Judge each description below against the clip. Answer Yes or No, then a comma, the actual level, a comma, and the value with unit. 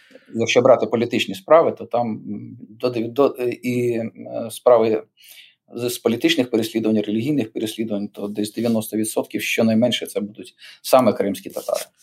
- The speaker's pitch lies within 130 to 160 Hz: No, low, 115 Hz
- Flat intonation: Yes, narrow, 1.9 semitones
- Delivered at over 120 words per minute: No, average, 110 wpm